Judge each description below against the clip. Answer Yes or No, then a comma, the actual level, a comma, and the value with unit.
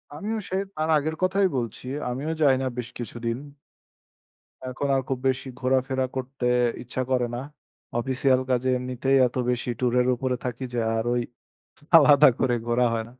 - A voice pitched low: Yes, low, 130 Hz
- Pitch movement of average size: No, narrow, 1.8 semitones